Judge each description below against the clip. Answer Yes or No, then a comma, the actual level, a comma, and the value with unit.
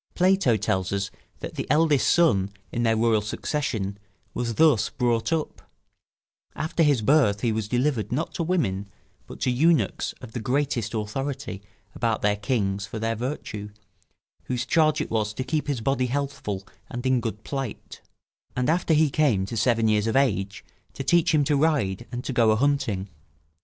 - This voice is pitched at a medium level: No, low, 120 Hz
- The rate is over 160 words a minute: Yes, average, 175 wpm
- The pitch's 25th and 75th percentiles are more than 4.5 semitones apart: Yes, average, 5.1 semitones